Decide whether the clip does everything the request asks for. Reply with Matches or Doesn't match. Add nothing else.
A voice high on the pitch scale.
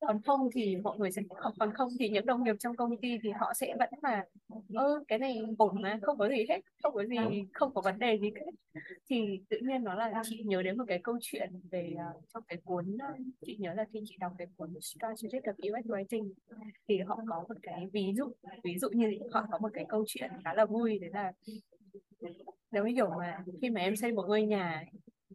Matches